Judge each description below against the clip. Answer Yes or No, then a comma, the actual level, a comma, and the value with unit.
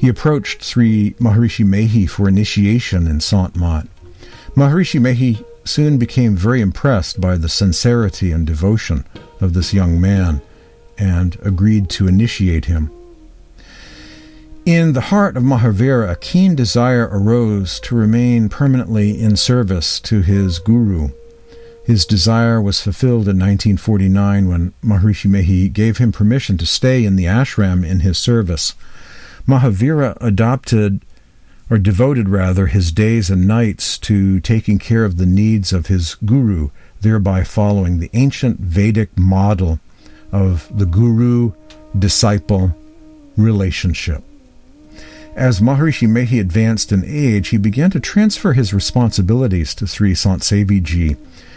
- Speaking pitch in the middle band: No, low, 105 Hz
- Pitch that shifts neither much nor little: Yes, average, 4.1 semitones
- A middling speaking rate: No, slow, 130 wpm